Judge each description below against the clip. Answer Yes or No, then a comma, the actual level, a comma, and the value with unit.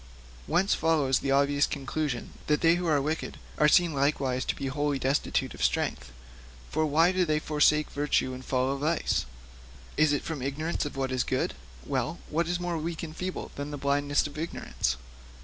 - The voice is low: No, medium, 150 Hz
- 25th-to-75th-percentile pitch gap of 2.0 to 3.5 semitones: Yes, average, 2.8 semitones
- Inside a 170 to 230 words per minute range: Yes, average, 185 wpm